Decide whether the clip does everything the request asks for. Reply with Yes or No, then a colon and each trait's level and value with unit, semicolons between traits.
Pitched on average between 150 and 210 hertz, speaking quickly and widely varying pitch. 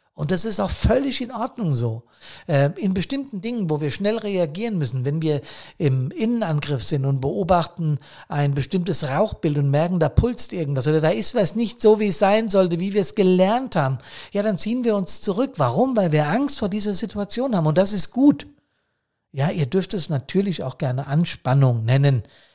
Yes: medium, 185 Hz; fast, 195 wpm; wide, 6.2 semitones